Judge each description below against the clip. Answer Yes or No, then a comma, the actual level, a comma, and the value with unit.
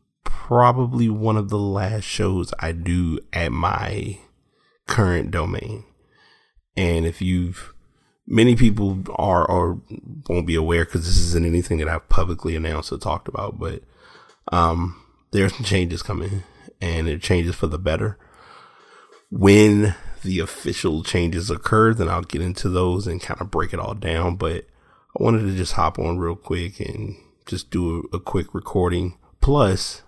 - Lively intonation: No, average, 3.7 semitones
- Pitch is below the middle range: Yes, very low, 90 Hz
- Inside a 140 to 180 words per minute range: Yes, average, 160 wpm